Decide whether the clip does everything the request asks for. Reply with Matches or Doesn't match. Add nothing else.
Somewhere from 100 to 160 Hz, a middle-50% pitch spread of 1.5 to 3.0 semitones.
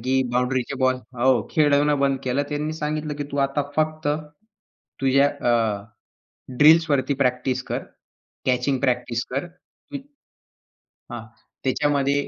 Matches